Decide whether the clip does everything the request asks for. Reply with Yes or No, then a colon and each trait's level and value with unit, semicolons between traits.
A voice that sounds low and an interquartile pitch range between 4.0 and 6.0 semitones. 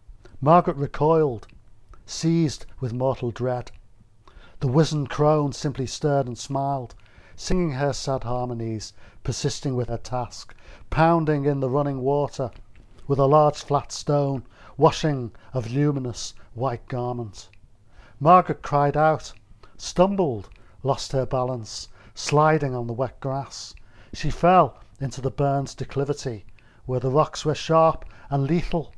Yes: low, 130 Hz; average, 4.6 semitones